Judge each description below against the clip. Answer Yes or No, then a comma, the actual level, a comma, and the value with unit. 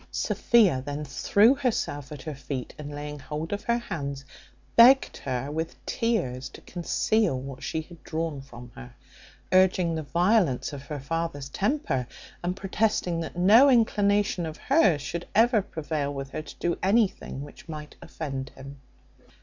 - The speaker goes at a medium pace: Yes, average, 160 wpm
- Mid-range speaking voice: Yes, medium, 160 Hz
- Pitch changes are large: Yes, wide, 6.4 semitones